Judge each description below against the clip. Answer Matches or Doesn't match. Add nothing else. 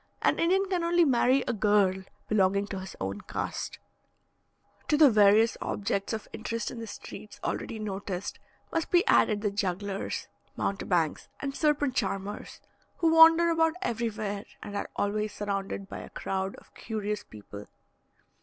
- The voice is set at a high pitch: Matches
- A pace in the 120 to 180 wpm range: Matches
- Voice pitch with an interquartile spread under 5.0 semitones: Doesn't match